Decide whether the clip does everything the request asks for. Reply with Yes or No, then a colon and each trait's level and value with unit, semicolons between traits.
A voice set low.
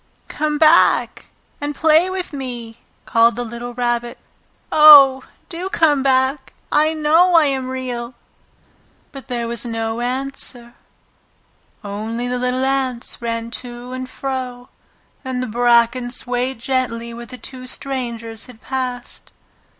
No: very high, 250 Hz